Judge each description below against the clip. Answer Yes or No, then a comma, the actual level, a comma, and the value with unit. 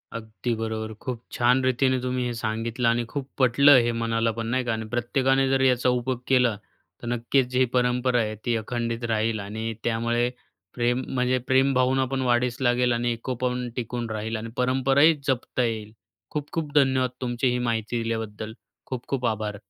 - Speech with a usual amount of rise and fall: No, narrow, 2.1 semitones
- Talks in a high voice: No, low, 120 Hz